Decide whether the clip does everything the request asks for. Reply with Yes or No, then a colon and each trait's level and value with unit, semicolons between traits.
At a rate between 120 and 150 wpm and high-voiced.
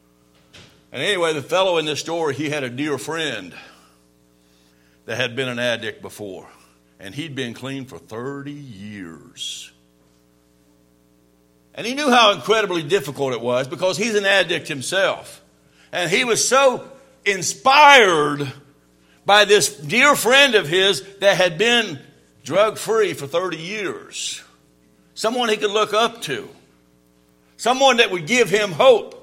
No: average, 140 wpm; medium, 150 Hz